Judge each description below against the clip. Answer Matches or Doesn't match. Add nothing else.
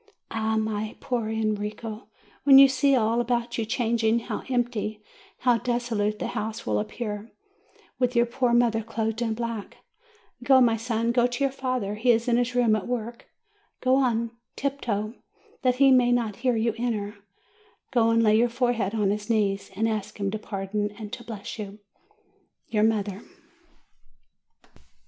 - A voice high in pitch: Matches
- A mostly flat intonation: Matches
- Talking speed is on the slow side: Doesn't match